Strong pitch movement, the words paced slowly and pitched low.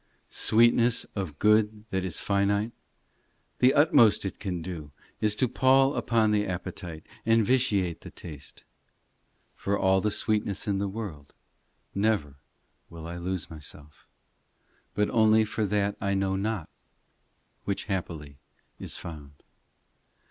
No: average, 3.9 semitones; slow, 130 wpm; low, 100 Hz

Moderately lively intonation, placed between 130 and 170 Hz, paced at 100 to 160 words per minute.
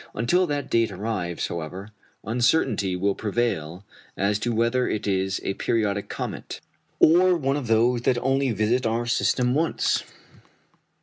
No: average, 4.1 semitones; low, 115 Hz; average, 140 wpm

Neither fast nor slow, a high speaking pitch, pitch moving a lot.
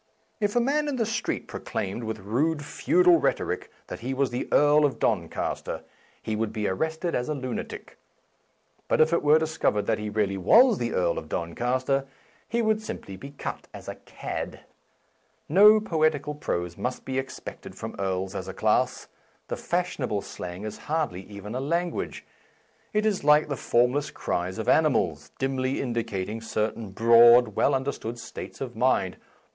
No: average, 185 wpm; low, 130 Hz; wide, 6.8 semitones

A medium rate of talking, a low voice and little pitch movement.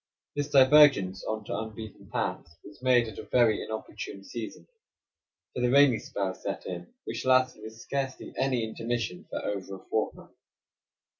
No: average, 155 wpm; low, 110 Hz; average, 4.0 semitones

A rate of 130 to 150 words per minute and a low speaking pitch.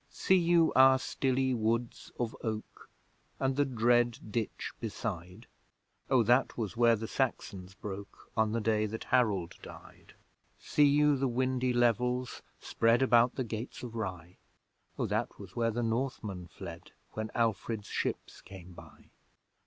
Yes: average, 145 wpm; low, 115 Hz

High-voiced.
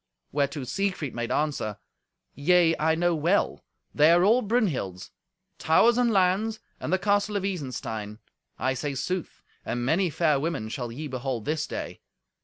No: medium, 160 Hz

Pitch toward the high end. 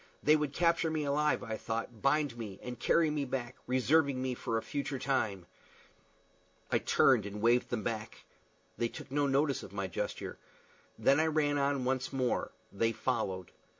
No: low, 130 Hz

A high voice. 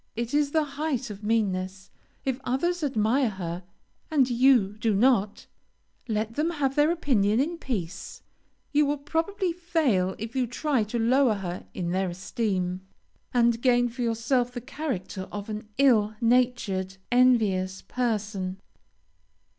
Yes: high, 235 Hz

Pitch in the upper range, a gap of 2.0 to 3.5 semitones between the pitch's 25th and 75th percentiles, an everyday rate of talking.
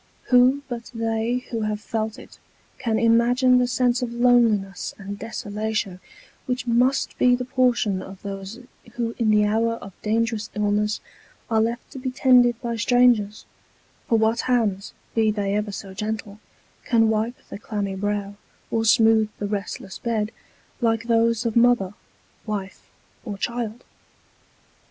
Yes: high, 225 Hz; narrow, 2.5 semitones; average, 145 wpm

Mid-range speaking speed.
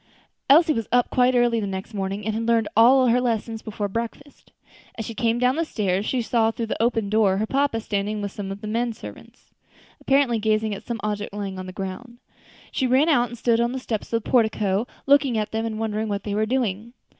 No: fast, 230 wpm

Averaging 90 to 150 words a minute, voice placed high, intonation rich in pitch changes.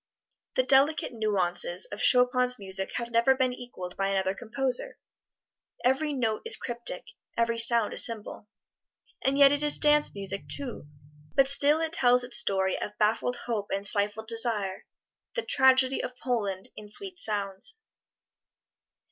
No: average, 145 wpm; high, 235 Hz; average, 4.5 semitones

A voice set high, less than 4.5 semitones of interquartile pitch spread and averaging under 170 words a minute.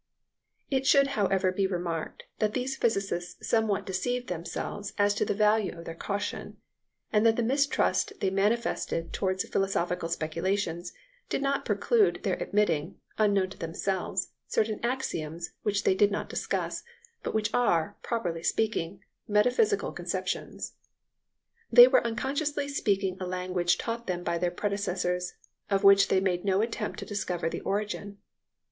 Yes: high, 200 Hz; average, 3.8 semitones; average, 145 wpm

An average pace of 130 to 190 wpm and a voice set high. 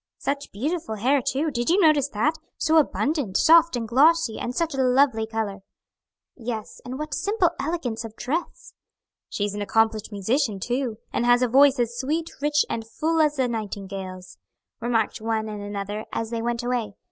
Yes: average, 175 wpm; high, 245 Hz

